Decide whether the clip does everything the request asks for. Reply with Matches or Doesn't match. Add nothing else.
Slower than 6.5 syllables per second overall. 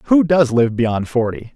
Matches